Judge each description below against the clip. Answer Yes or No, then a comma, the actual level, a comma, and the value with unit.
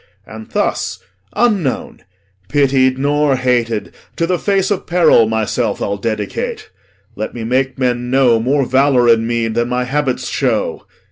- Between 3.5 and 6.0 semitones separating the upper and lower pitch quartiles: Yes, average, 3.8 semitones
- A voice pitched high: No, low, 130 Hz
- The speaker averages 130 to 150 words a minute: Yes, average, 145 wpm